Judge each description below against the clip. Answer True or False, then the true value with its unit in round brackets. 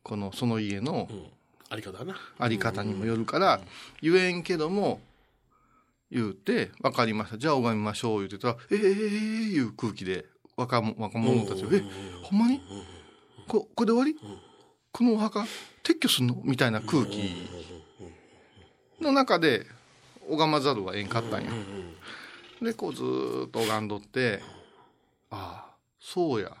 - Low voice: True (120 Hz)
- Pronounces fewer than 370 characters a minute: True (270 characters per minute)